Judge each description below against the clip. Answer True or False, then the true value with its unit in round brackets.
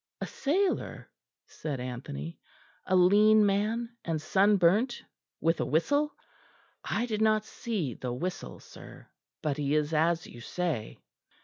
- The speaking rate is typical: False (130 wpm)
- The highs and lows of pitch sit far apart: True (6.3 semitones)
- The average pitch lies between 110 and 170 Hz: False (180 Hz)